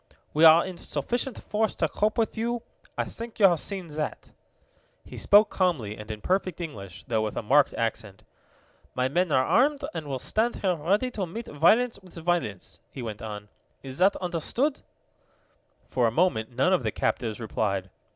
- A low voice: No, medium, 165 Hz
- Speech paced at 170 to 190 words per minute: Yes, average, 180 wpm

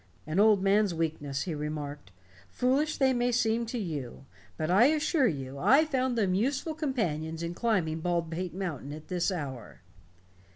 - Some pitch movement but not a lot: No, wide, 7.8 semitones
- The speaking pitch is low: No, medium, 185 Hz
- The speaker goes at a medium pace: Yes, average, 160 wpm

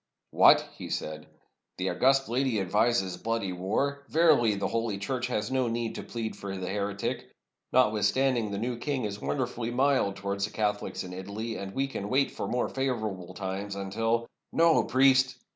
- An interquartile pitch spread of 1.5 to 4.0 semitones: No, average, 4.4 semitones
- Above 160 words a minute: Yes, average, 180 wpm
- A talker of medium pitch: No, low, 115 Hz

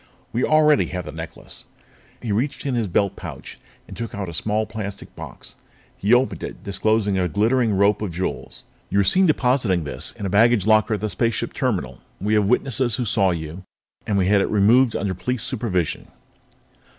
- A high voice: No, low, 105 Hz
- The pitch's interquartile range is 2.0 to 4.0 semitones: Yes, average, 3.6 semitones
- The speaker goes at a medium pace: Yes, average, 190 wpm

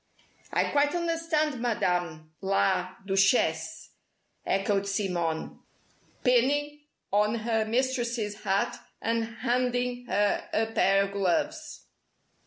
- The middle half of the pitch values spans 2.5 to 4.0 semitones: No, average, 4.4 semitones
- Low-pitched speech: No, high, 220 Hz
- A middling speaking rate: No, slow, 95 wpm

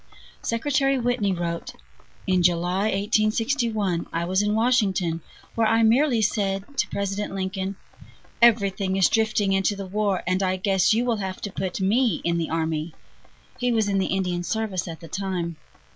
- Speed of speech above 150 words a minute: Yes, average, 165 wpm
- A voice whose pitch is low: No, high, 195 Hz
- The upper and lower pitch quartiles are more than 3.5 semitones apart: No, average, 3.1 semitones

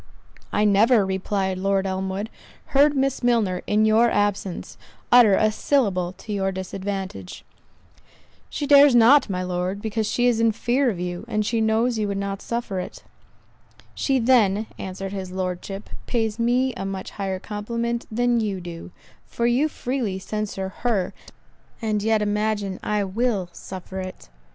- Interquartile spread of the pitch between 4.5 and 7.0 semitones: No, average, 3.6 semitones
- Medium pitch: No, high, 210 Hz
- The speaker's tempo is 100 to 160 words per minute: Yes, average, 155 wpm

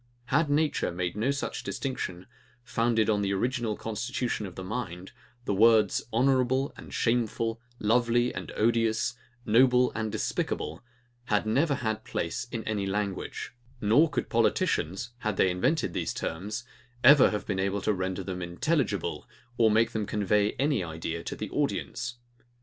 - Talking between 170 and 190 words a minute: No, average, 150 wpm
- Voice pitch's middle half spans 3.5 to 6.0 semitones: Yes, average, 3.8 semitones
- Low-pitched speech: Yes, low, 110 Hz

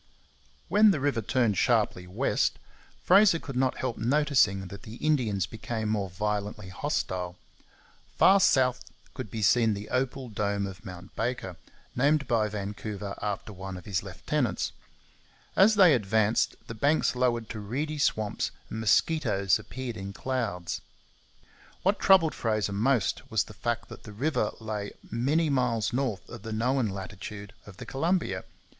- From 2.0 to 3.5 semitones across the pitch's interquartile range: No, average, 4.6 semitones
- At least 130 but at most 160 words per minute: Yes, average, 150 wpm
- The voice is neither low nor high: No, low, 110 Hz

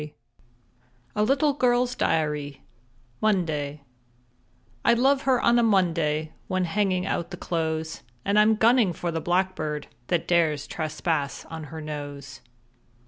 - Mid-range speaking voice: Yes, medium, 170 Hz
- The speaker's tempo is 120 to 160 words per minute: Yes, slow, 135 wpm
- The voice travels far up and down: Yes, wide, 5.7 semitones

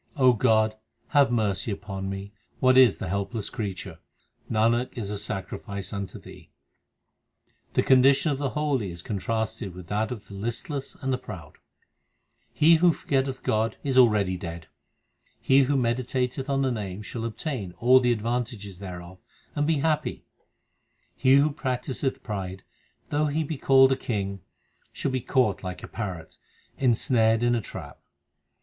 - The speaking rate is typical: Yes, average, 160 wpm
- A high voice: No, low, 115 Hz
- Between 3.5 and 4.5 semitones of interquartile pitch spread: No, average, 4.9 semitones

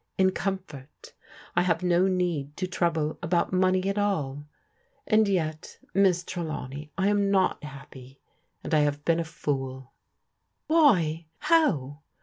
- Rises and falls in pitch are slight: No, average, 4.3 semitones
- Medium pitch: Yes, medium, 170 Hz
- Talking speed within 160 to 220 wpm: No, average, 140 wpm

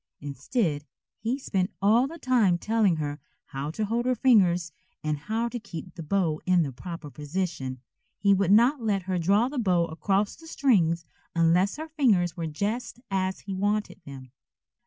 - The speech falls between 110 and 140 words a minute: No, average, 175 wpm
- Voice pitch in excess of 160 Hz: Yes, high, 190 Hz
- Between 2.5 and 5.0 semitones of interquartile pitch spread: No, wide, 5.4 semitones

